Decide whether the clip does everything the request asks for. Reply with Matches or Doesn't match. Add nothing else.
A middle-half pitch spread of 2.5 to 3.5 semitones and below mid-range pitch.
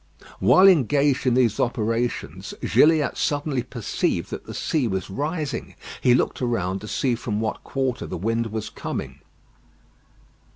Doesn't match